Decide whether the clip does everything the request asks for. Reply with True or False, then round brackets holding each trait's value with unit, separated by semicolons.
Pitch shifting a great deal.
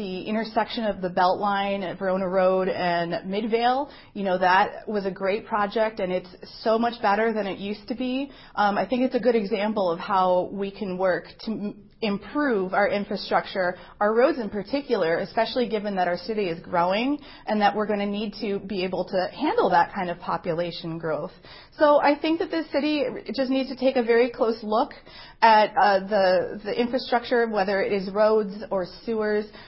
False (3.8 semitones)